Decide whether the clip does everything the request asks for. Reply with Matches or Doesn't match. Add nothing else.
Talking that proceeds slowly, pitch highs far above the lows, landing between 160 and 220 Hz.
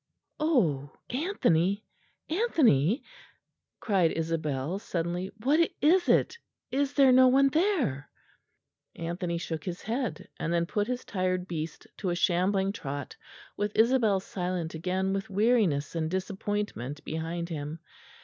Matches